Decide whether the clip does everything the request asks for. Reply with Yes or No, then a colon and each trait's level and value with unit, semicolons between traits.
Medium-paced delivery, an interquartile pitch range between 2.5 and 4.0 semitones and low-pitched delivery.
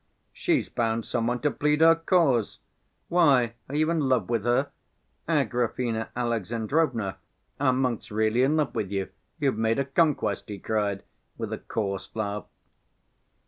No: average, 150 wpm; average, 4.7 semitones; low, 120 Hz